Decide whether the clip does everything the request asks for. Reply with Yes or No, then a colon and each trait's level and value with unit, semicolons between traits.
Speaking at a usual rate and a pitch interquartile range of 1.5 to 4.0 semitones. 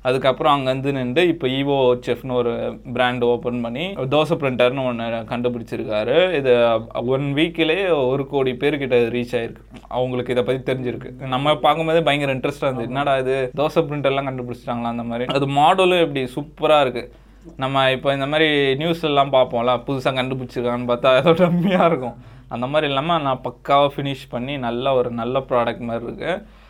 No: fast, 155 wpm; narrow, 2.6 semitones